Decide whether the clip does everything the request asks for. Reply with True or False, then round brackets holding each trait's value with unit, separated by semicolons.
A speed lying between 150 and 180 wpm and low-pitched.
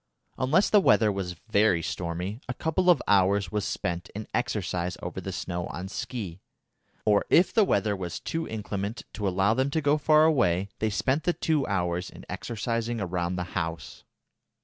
True (175 wpm; 105 Hz)